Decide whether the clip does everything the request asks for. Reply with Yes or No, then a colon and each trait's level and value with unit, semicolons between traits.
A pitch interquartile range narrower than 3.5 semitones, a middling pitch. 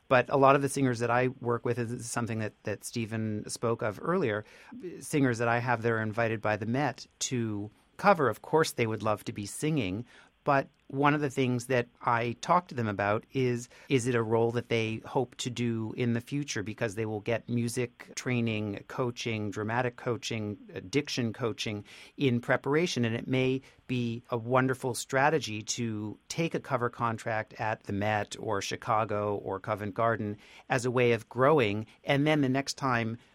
No: average, 2.9 semitones; low, 120 Hz